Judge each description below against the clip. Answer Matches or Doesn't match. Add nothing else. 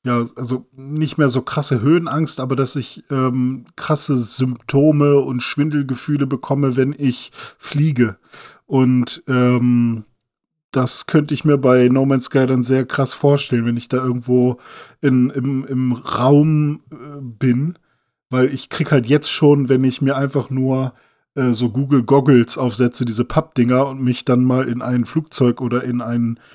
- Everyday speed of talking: Matches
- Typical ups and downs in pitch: Doesn't match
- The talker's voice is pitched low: Matches